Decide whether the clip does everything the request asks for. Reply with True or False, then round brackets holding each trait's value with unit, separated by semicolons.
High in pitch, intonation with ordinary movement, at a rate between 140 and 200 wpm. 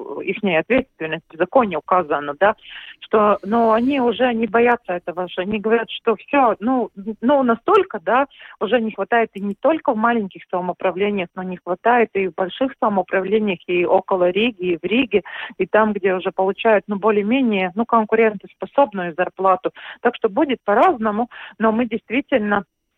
True (210 Hz; 4.1 semitones; 160 wpm)